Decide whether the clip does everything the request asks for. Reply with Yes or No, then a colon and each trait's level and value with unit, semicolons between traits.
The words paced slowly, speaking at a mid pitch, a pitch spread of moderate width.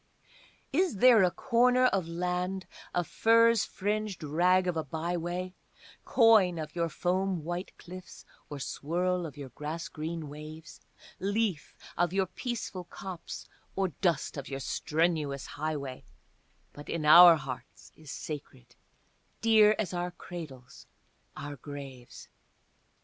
Yes: slow, 130 wpm; medium, 175 Hz; average, 3.9 semitones